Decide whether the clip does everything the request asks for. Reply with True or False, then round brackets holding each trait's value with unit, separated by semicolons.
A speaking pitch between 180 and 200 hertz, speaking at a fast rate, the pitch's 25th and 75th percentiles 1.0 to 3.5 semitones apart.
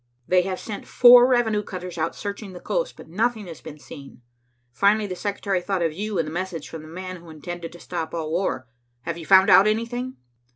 False (185 Hz; 215 wpm; 4.0 semitones)